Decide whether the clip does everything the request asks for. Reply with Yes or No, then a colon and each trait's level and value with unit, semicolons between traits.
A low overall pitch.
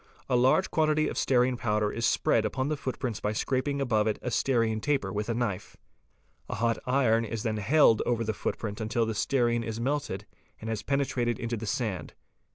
Yes: low, 115 Hz